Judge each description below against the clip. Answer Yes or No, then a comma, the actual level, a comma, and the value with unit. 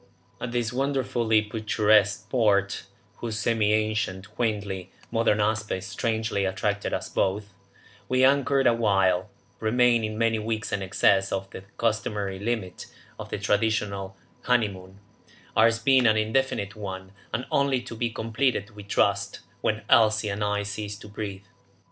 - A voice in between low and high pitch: No, low, 110 Hz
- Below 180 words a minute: Yes, slow, 135 wpm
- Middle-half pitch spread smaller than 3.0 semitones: Yes, narrow, 2.4 semitones